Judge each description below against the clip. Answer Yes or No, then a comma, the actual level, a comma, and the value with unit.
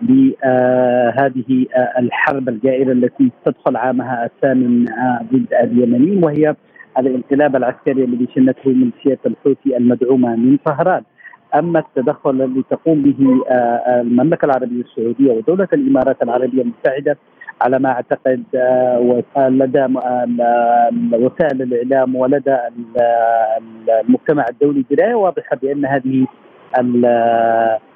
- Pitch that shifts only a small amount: Yes, narrow, 2.0 semitones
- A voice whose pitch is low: Yes, low, 130 Hz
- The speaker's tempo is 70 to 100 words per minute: No, average, 115 wpm